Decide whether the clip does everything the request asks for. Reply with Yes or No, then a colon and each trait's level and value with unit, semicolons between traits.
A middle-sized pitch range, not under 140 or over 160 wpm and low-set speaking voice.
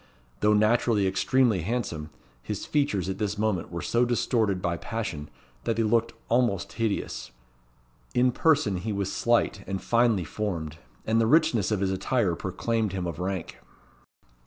Yes: average, 3.9 semitones; average, 155 wpm; low, 105 Hz